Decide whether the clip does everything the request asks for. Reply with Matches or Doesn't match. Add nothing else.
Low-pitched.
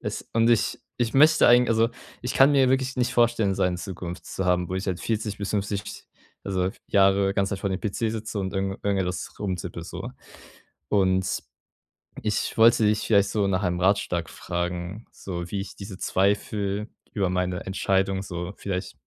Matches